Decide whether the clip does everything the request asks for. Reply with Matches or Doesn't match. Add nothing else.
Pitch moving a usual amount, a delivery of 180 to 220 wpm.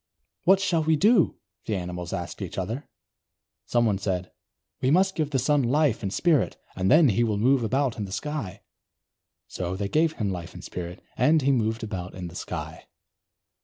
Doesn't match